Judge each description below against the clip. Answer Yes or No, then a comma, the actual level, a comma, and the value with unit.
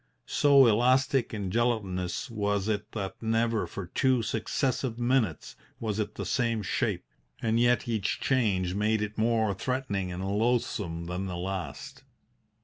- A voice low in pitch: Yes, low, 110 Hz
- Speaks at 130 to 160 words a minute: Yes, average, 145 wpm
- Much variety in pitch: No, average, 3.7 semitones